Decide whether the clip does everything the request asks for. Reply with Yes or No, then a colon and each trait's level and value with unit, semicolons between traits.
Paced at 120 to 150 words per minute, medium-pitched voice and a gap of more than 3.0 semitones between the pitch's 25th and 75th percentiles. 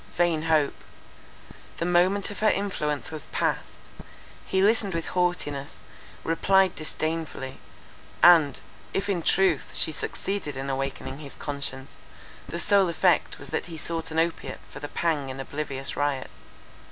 Yes: average, 140 wpm; medium, 160 Hz; average, 3.9 semitones